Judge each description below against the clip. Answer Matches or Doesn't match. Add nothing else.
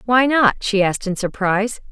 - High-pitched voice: Matches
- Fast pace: Doesn't match